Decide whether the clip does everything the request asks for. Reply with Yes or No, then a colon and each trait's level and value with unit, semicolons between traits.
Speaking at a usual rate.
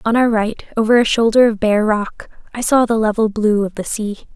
No: fast, 235 wpm